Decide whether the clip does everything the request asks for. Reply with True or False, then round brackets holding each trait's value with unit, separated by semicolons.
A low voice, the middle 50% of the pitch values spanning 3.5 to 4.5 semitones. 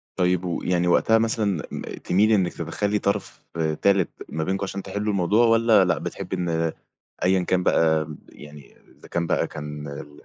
True (90 Hz; 3.9 semitones)